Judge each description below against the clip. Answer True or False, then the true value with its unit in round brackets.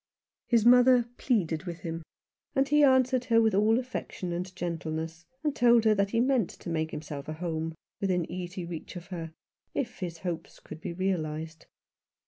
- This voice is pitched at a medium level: True (180 Hz)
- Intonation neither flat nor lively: False (6.1 semitones)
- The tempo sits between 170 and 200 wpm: True (175 wpm)